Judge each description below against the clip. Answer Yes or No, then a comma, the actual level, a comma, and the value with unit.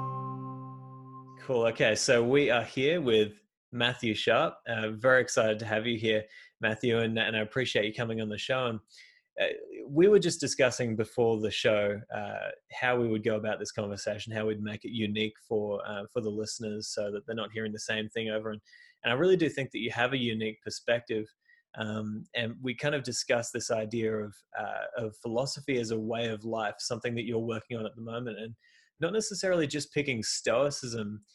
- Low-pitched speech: Yes, low, 115 Hz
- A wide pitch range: No, average, 3.2 semitones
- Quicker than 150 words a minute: Yes, average, 200 wpm